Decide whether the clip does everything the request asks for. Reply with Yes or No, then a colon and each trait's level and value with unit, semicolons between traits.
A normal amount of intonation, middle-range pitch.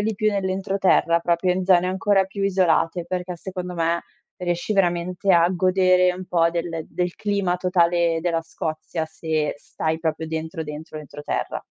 No: narrow, 2.1 semitones; medium, 175 Hz